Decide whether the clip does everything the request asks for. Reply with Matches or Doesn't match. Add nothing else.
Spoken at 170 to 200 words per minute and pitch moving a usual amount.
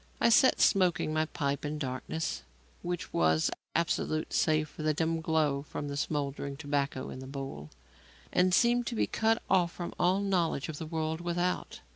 Matches